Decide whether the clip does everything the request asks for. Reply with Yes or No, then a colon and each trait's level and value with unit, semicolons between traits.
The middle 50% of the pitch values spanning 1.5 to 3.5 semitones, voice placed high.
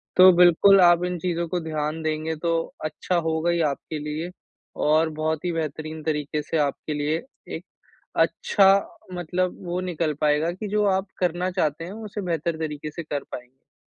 No: narrow, 2.6 semitones; medium, 165 Hz